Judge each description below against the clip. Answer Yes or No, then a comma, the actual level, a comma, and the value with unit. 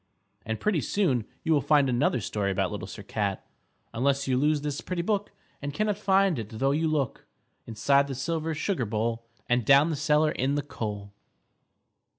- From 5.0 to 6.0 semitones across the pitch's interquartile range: Yes, wide, 5.4 semitones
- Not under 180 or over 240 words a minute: Yes, average, 185 wpm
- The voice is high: No, medium, 140 Hz